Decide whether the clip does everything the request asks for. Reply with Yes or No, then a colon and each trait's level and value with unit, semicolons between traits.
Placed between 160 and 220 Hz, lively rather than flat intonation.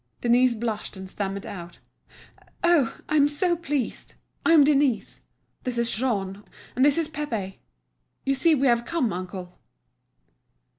No: high, 245 Hz; wide, 6.4 semitones